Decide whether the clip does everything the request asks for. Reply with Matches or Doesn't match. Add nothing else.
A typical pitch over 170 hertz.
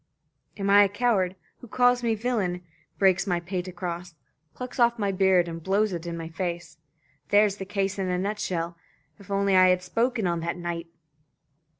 Matches